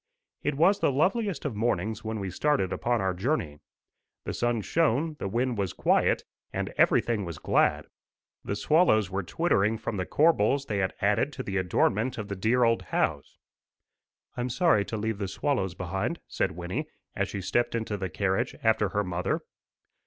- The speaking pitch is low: Yes, low, 110 Hz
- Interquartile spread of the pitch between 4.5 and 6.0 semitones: Yes, average, 5.1 semitones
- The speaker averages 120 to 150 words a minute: No, average, 175 wpm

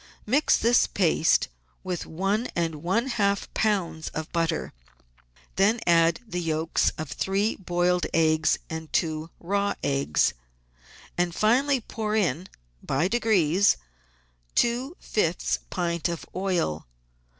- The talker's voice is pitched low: No, medium, 180 Hz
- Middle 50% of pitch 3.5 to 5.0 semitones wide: Yes, average, 4.6 semitones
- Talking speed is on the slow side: Yes, slow, 115 wpm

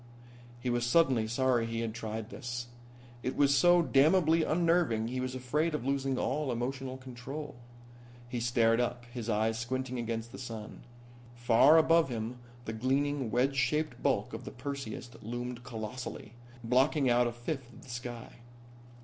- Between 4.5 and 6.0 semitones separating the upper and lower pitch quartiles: No, average, 2.7 semitones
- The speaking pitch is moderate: No, low, 125 Hz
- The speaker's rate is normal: Yes, average, 160 wpm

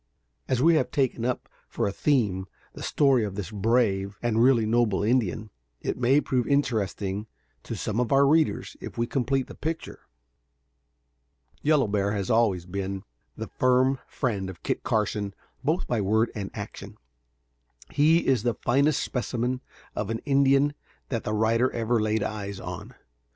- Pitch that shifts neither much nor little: Yes, average, 4.3 semitones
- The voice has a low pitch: Yes, low, 115 Hz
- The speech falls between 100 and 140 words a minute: No, average, 160 wpm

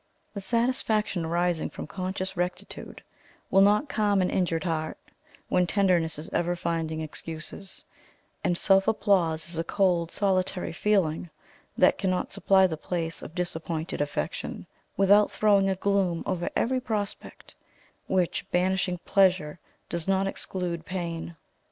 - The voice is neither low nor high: Yes, medium, 180 Hz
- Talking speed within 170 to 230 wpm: No, slow, 135 wpm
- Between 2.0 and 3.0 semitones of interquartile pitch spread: Yes, average, 2.7 semitones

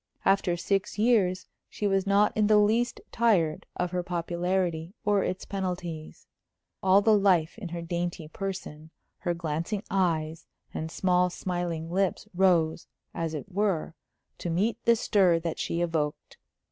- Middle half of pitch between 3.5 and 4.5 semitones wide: No, average, 2.9 semitones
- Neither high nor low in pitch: Yes, medium, 180 Hz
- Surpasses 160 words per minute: No, average, 145 wpm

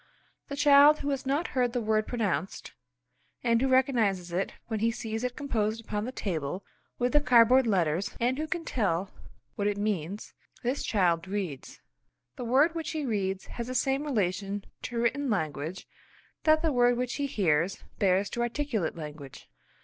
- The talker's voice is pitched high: Yes, high, 230 Hz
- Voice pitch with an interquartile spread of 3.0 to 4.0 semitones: No, wide, 5.4 semitones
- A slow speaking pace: No, average, 170 wpm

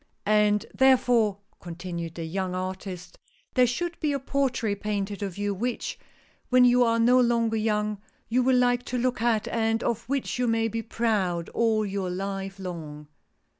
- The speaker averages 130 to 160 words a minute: No, average, 170 wpm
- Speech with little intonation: No, average, 4.1 semitones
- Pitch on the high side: Yes, high, 220 Hz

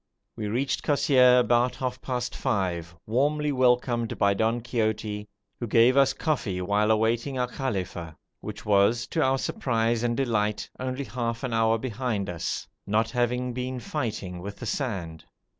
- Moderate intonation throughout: Yes, average, 3.3 semitones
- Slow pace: No, average, 155 wpm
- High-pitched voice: No, low, 120 Hz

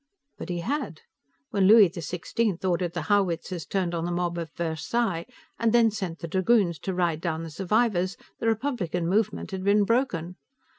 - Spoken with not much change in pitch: No, average, 4.0 semitones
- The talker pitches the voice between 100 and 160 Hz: No, medium, 185 Hz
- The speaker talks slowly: No, average, 170 wpm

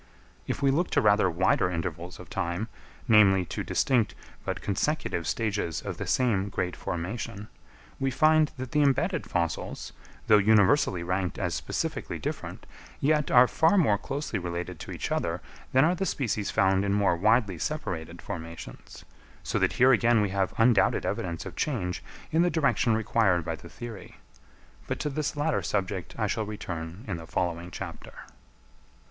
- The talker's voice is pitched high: No, low, 105 Hz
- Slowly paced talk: No, average, 165 wpm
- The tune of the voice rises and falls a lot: Yes, wide, 6.4 semitones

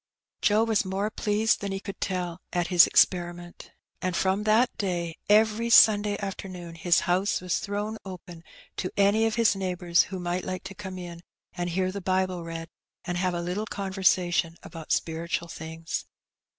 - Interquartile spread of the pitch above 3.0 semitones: No, average, 2.7 semitones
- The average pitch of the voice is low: No, medium, 185 Hz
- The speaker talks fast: No, average, 175 wpm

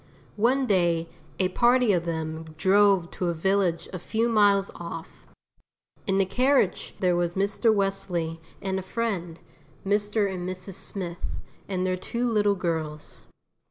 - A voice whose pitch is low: No, high, 190 Hz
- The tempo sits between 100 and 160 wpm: Yes, average, 145 wpm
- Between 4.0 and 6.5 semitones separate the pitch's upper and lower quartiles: No, average, 3.1 semitones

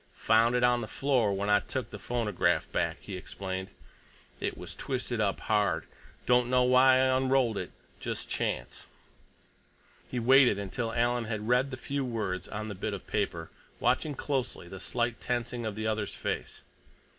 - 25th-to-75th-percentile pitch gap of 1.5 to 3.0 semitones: No, average, 3.4 semitones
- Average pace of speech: Yes, average, 170 wpm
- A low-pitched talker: Yes, low, 115 Hz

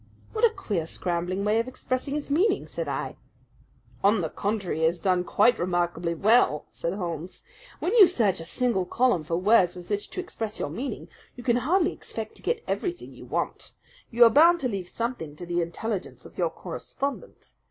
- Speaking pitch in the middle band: No, high, 210 Hz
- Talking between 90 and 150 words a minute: No, average, 195 wpm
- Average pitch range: No, wide, 6.5 semitones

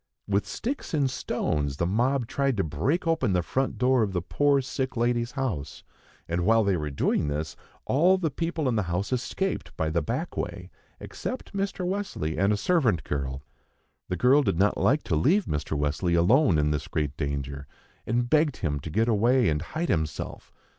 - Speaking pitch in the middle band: No, low, 110 Hz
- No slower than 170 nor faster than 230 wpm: Yes, average, 190 wpm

